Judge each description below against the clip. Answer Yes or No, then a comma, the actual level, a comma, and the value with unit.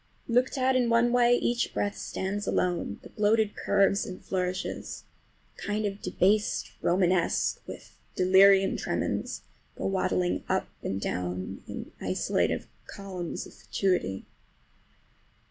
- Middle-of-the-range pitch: No, high, 195 Hz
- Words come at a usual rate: No, slow, 115 wpm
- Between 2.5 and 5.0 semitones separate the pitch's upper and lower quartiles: Yes, average, 2.9 semitones